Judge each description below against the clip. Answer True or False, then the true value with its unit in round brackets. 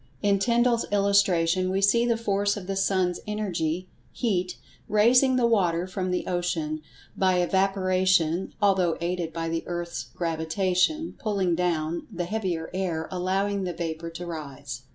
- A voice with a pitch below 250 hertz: True (185 Hz)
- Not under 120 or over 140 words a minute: True (135 wpm)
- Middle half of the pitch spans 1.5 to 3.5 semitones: True (2.9 semitones)